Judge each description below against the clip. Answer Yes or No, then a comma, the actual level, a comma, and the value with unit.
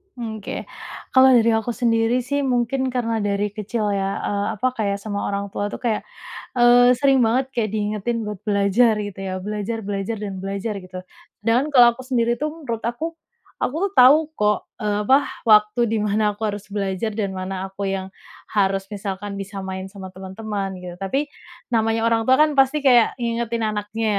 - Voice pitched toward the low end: No, high, 215 Hz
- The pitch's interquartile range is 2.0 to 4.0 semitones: Yes, average, 3.2 semitones